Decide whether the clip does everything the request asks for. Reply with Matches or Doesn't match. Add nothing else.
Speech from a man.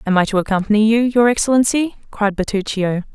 Doesn't match